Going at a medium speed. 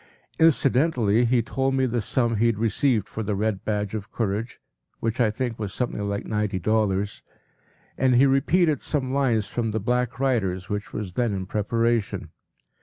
Yes: average, 180 wpm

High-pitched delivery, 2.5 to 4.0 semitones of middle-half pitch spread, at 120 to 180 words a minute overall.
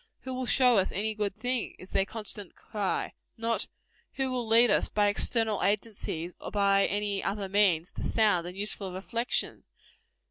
Yes: high, 210 Hz; average, 2.8 semitones; average, 170 wpm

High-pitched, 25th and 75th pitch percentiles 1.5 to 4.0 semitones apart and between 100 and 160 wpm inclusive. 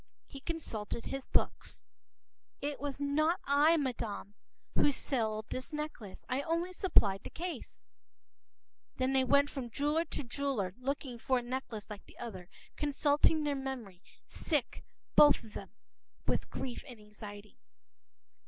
No: very high, 270 Hz; average, 4.8 semitones; slow, 135 wpm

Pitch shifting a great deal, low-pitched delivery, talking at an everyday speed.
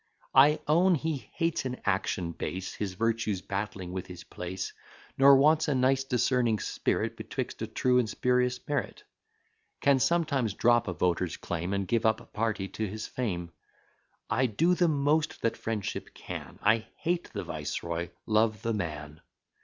Yes: wide, 6.1 semitones; low, 115 Hz; average, 160 wpm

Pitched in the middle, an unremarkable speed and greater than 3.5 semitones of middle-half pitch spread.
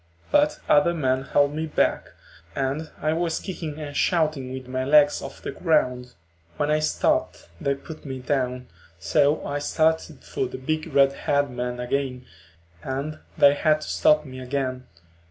No: medium, 145 Hz; average, 165 wpm; average, 3.0 semitones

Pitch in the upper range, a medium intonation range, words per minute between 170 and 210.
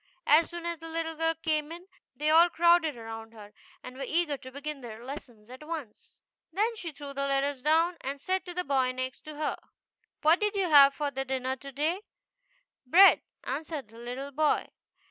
Yes: very high, 295 Hz; average, 3.9 semitones; average, 195 wpm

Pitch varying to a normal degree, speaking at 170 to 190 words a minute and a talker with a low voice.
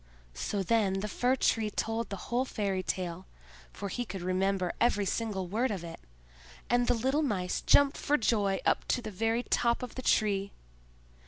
No: average, 3.9 semitones; average, 180 wpm; high, 210 Hz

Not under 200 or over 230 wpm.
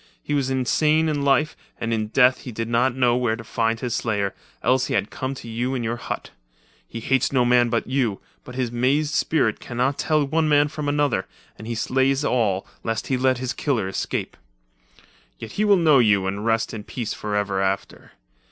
Yes: fast, 205 wpm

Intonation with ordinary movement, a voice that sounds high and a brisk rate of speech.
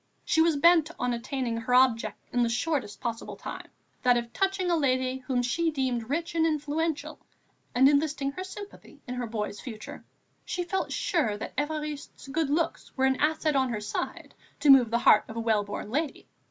No: average, 4.8 semitones; very high, 270 Hz; average, 195 wpm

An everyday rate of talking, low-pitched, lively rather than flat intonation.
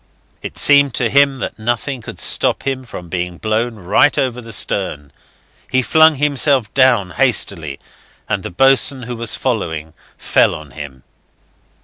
Yes: average, 150 wpm; low, 120 Hz; wide, 7.0 semitones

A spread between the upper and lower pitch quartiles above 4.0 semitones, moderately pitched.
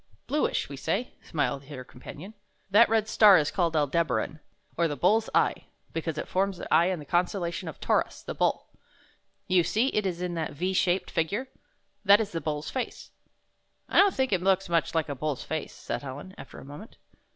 Yes: average, 4.5 semitones; medium, 175 Hz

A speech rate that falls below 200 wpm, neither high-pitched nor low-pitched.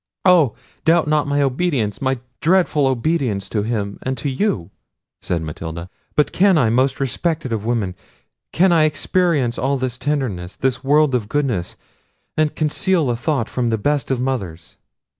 No: average, 160 wpm; low, 130 Hz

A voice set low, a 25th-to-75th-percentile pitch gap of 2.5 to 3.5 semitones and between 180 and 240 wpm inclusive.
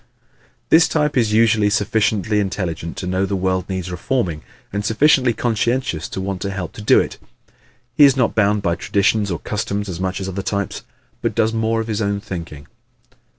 Yes: low, 100 Hz; average, 3.2 semitones; average, 190 wpm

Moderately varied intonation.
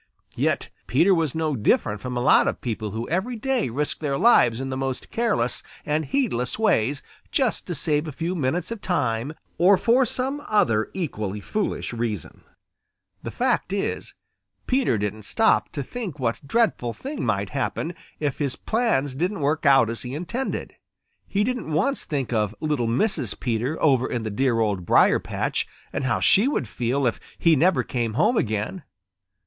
No: wide, 8.4 semitones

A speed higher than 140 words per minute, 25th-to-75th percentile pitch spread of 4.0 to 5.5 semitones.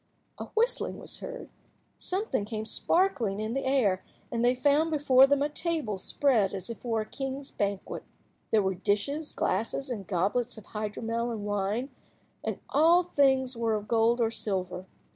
Yes: average, 170 wpm; average, 5.2 semitones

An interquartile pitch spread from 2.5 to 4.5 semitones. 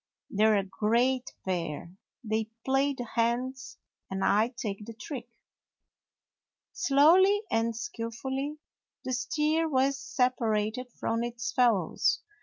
Yes: average, 3.6 semitones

